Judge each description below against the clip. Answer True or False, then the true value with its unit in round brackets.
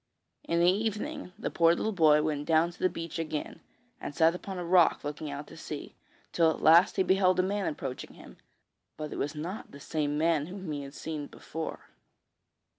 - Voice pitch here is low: False (165 Hz)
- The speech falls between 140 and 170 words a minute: False (200 wpm)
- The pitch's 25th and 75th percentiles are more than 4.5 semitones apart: False (3.3 semitones)